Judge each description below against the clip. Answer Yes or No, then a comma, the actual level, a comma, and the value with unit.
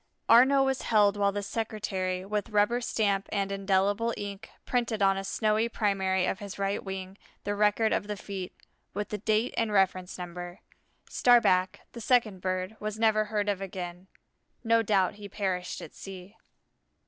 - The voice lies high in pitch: Yes, high, 205 Hz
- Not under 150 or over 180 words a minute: Yes, average, 165 wpm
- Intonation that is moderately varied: No, narrow, 2.2 semitones